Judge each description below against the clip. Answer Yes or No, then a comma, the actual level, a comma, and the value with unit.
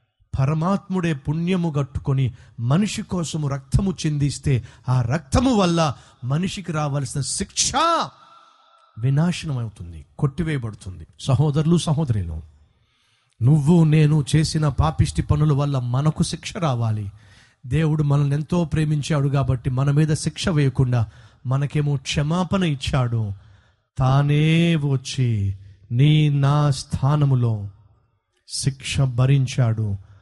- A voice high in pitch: No, medium, 140 Hz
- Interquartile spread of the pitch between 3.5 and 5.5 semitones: Yes, average, 4.6 semitones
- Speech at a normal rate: Yes, average, 90 wpm